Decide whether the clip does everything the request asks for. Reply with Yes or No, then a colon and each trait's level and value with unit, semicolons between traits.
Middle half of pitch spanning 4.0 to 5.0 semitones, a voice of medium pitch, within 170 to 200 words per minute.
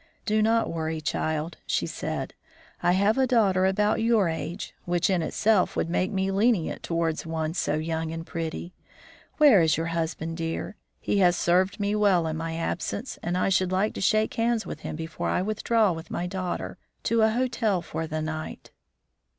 Yes: average, 4.4 semitones; medium, 180 Hz; average, 185 wpm